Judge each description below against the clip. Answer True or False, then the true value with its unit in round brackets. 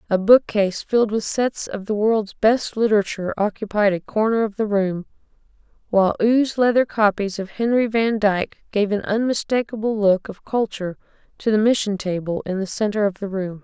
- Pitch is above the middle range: True (210 Hz)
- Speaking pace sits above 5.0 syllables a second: True (5.4 syllables/s)